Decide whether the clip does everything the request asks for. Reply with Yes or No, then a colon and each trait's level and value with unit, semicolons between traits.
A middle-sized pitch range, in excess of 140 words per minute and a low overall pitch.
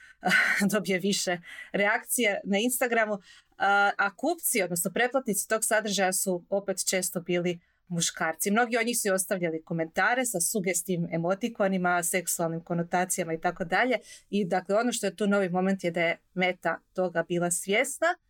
No: average, 3.2 semitones; average, 150 wpm; high, 190 Hz